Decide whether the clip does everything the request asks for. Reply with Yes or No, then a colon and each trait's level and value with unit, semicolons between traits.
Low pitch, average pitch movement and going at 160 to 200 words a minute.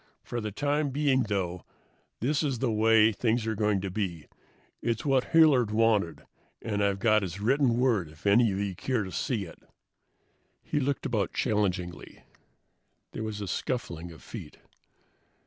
Yes: low, 110 Hz; average, 4.3 semitones; average, 165 wpm